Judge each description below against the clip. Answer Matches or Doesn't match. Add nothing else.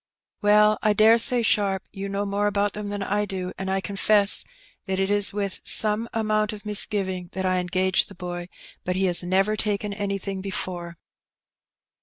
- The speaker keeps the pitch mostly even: Matches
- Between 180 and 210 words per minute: Matches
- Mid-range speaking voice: Doesn't match